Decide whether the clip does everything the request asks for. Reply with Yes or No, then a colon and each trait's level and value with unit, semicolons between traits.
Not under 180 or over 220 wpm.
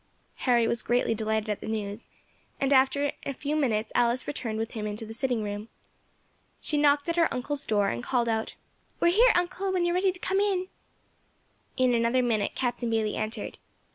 Yes: average, 200 wpm